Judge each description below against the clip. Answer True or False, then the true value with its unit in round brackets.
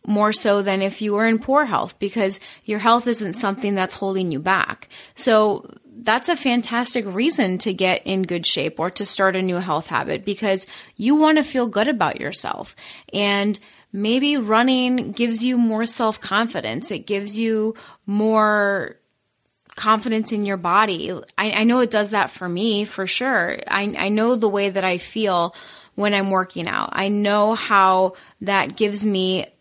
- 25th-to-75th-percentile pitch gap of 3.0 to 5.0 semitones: False (2.6 semitones)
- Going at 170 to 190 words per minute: True (175 wpm)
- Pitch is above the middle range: True (210 Hz)